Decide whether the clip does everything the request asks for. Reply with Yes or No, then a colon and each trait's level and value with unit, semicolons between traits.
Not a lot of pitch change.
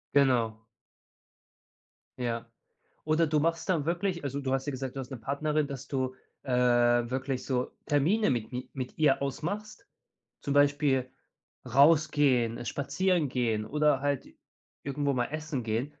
No: average, 3.2 semitones